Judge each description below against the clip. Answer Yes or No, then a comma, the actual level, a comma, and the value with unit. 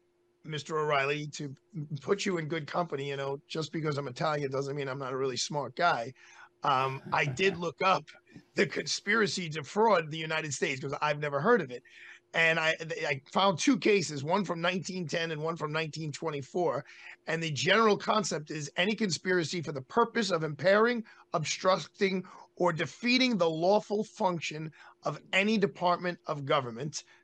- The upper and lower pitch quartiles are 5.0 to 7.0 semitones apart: No, average, 4.2 semitones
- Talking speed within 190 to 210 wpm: No, average, 165 wpm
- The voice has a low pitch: No, medium, 165 Hz